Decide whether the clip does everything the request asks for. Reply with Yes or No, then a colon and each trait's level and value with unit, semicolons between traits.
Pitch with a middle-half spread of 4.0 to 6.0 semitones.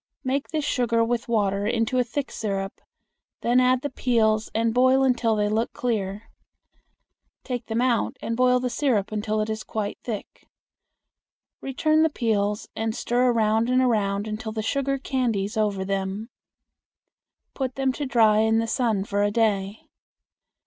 No: average, 2.9 semitones